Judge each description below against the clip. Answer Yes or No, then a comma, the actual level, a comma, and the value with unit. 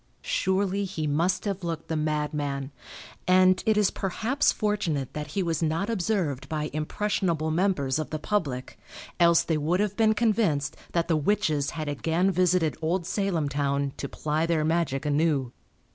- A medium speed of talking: Yes, average, 160 wpm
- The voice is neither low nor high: Yes, medium, 165 Hz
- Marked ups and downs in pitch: No, average, 4.2 semitones